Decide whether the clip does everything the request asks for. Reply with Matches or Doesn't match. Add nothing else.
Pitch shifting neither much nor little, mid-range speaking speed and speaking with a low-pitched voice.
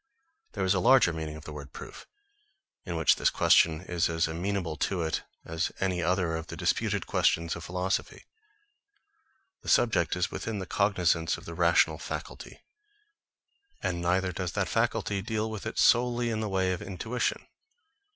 Matches